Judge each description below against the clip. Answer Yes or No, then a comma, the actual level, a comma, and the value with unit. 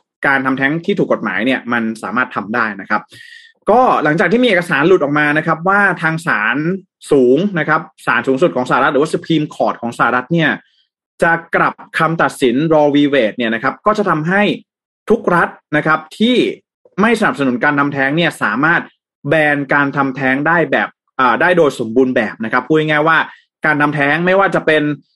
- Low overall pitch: No, medium, 155 Hz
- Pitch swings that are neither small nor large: Yes, average, 4.6 semitones